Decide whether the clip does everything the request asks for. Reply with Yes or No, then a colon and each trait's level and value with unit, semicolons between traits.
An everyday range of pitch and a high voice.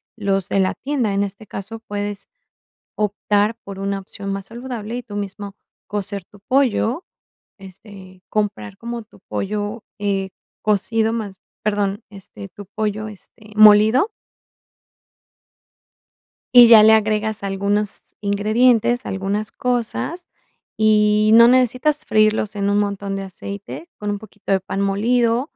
No: narrow, 2.2 semitones; high, 210 Hz